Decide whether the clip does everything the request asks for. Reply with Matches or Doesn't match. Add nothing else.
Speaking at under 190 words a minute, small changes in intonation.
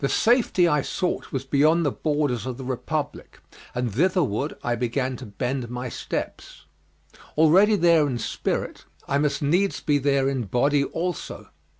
Doesn't match